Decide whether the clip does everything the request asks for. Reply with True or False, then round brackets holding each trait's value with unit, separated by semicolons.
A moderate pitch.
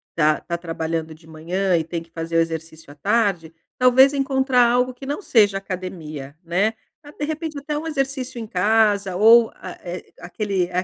False (195 Hz)